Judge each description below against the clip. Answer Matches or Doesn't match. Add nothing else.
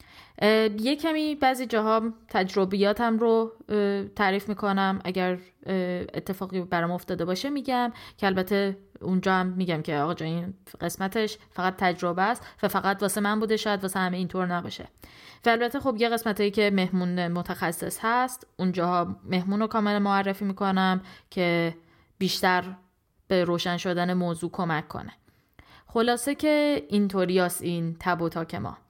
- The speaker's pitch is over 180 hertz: Matches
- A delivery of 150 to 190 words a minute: Doesn't match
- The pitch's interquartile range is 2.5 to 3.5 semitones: Matches